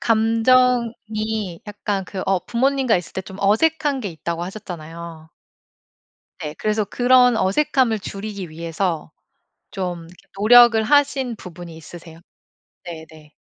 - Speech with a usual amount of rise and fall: No, wide, 5.7 semitones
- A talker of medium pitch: No, high, 205 Hz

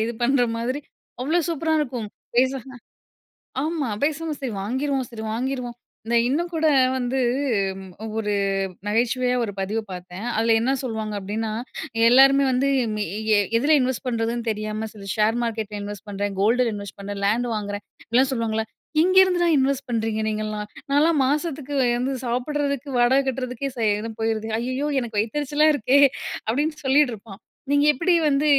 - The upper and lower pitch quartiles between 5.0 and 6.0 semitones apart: No, average, 4.1 semitones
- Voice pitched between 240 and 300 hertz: Yes, high, 245 Hz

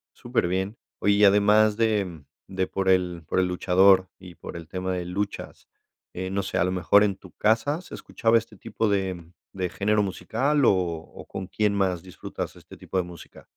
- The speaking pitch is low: Yes, very low, 95 Hz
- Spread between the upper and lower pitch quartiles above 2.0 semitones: Yes, narrow, 2.4 semitones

